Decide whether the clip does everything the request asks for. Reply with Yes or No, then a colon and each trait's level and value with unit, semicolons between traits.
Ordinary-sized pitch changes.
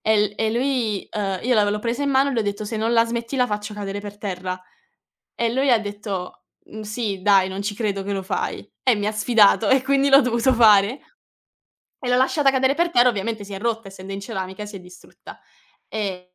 Yes: average, 3.3 semitones